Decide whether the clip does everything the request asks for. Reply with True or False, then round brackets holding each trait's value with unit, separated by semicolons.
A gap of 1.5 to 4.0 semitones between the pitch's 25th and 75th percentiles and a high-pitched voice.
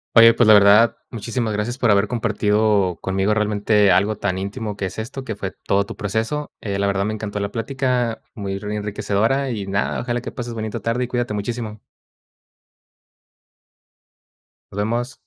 False (2.6 semitones; 105 Hz)